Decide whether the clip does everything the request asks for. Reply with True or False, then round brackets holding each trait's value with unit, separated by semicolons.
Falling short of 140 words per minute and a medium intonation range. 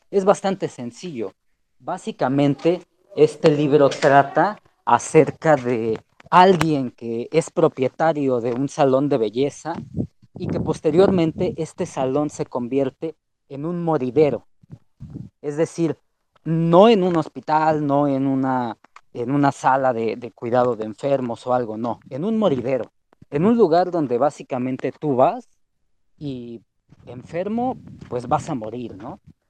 True (130 wpm; 4.3 semitones)